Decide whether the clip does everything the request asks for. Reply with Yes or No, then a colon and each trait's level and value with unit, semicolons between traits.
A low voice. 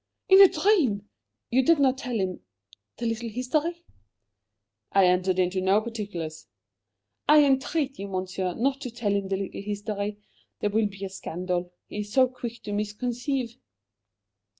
No: high, 210 Hz